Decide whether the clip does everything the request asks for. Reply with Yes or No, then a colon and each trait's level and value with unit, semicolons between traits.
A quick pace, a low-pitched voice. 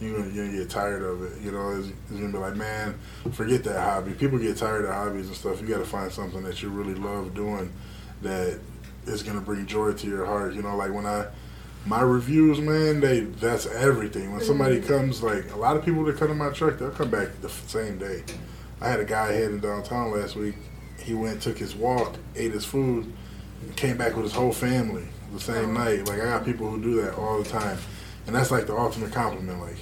Yes: fast, 230 wpm; low, 105 Hz